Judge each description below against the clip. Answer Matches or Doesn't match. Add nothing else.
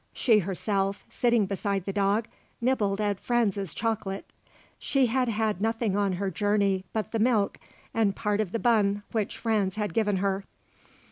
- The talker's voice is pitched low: Doesn't match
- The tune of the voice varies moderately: Doesn't match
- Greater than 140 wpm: Matches